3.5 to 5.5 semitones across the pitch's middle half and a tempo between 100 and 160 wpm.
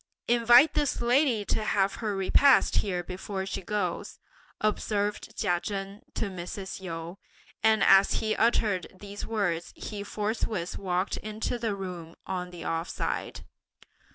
No: average, 3.0 semitones; average, 140 wpm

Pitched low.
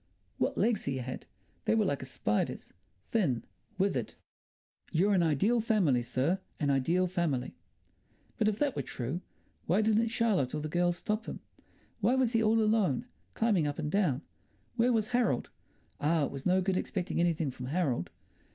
No: medium, 180 Hz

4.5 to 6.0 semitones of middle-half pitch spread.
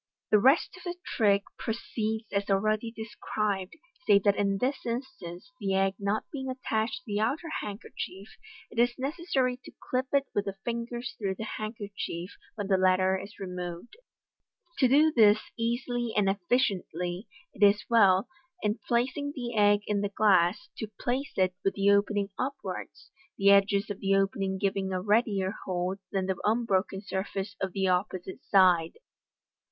No: average, 3.6 semitones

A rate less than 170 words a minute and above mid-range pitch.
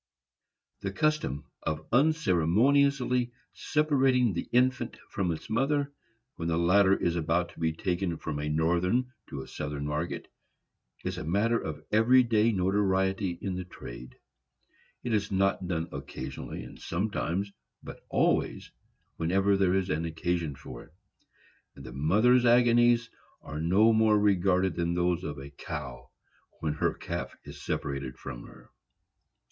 No: average, 140 wpm; very low, 95 Hz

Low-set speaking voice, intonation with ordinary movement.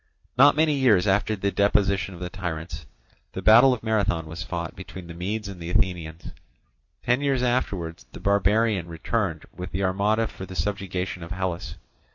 Yes: very low, 95 Hz; average, 3.9 semitones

